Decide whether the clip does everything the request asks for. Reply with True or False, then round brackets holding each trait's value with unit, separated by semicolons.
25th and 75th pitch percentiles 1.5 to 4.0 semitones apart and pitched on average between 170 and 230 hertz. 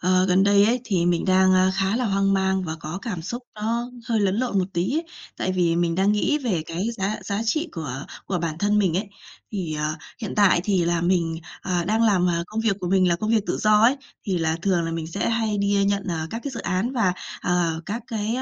True (3.6 semitones; 190 Hz)